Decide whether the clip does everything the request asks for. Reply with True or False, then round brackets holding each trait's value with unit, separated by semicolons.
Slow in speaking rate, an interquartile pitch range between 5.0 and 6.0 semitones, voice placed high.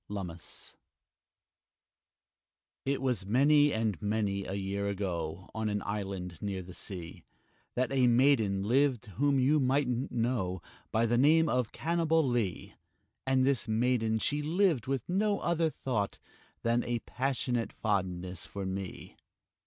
False (130 wpm; 5.5 semitones; 115 Hz)